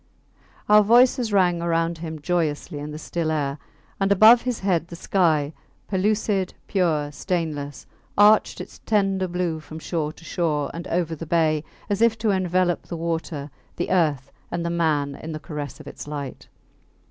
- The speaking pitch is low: No, medium, 170 Hz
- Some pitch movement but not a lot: Yes, average, 3.7 semitones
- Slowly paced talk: No, average, 170 wpm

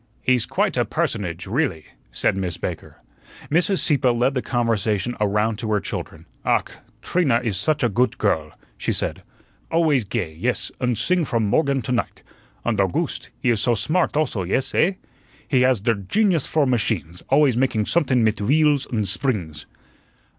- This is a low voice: Yes, low, 120 Hz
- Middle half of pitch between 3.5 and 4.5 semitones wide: No, average, 5.2 semitones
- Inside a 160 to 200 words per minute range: Yes, average, 170 wpm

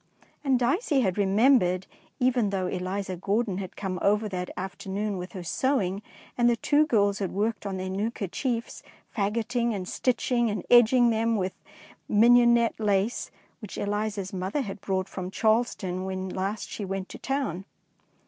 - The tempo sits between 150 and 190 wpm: Yes, average, 160 wpm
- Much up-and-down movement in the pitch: No, average, 3.8 semitones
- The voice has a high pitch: Yes, high, 205 Hz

